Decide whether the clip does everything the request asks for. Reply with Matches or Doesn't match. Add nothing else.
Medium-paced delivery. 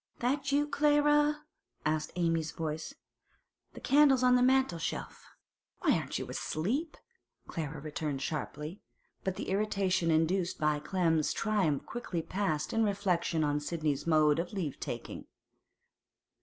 Doesn't match